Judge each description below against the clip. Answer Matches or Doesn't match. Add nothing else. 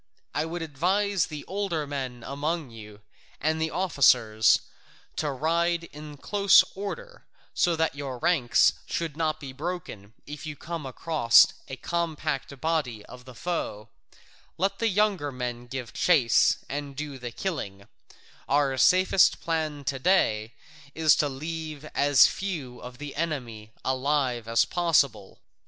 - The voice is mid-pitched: Matches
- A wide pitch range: Doesn't match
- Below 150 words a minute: Matches